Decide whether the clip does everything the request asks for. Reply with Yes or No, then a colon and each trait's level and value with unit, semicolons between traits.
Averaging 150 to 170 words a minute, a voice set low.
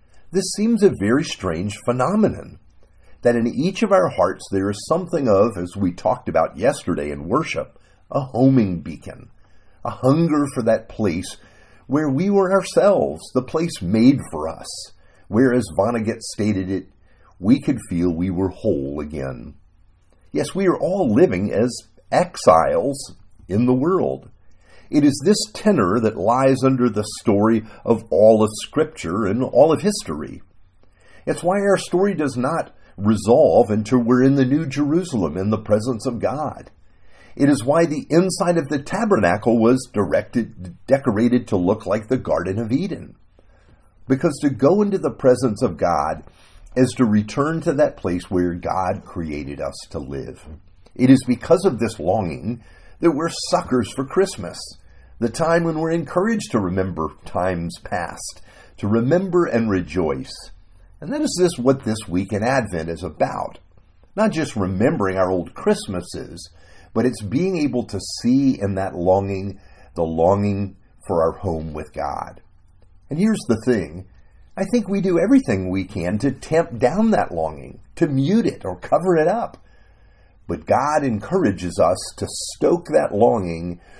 Yes: average, 160 wpm; low, 110 Hz